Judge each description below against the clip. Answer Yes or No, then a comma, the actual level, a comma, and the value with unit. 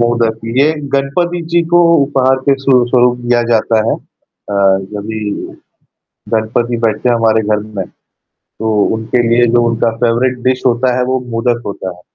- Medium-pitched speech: No, low, 120 Hz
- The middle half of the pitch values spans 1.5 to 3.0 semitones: Yes, narrow, 2.4 semitones